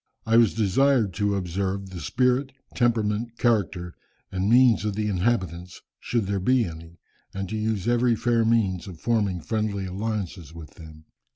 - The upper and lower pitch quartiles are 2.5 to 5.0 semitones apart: Yes, average, 4.0 semitones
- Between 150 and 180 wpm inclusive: Yes, average, 160 wpm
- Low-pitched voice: Yes, low, 105 Hz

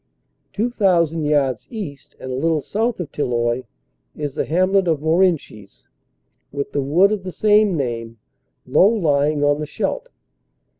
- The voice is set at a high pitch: No, medium, 155 Hz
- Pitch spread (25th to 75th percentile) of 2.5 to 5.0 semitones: No, wide, 5.4 semitones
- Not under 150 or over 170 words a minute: Yes, average, 155 wpm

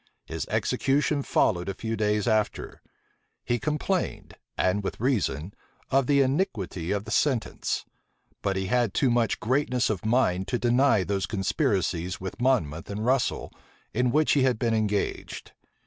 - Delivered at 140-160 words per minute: Yes, average, 150 wpm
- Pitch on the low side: Yes, low, 110 Hz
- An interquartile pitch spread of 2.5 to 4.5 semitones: No, average, 5.0 semitones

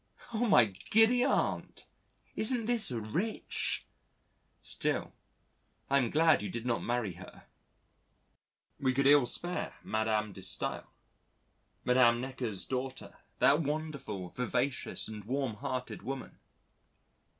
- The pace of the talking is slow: Yes, slow, 110 wpm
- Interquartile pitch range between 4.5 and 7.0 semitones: Yes, average, 5.2 semitones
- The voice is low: Yes, low, 130 Hz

